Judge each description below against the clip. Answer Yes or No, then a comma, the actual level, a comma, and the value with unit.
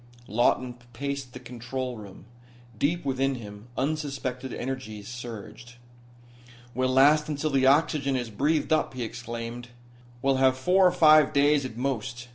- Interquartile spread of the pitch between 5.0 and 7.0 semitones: No, average, 2.8 semitones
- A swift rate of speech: No, average, 140 wpm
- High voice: No, low, 130 Hz